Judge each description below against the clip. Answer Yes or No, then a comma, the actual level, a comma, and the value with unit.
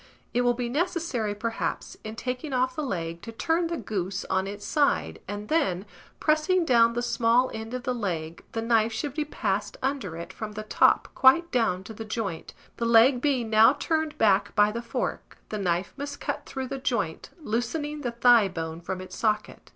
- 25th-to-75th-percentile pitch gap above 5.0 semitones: No, average, 4.5 semitones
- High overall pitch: Yes, high, 230 Hz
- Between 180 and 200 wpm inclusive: Yes, average, 195 wpm